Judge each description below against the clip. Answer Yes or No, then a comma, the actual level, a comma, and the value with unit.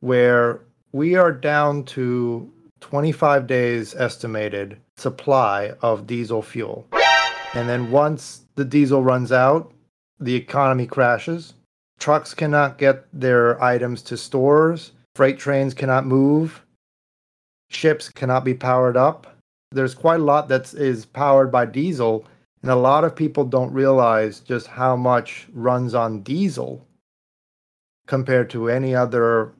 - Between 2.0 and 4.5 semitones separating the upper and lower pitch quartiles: Yes, average, 2.9 semitones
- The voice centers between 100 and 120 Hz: No, low, 130 Hz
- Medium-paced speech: No, slow, 130 wpm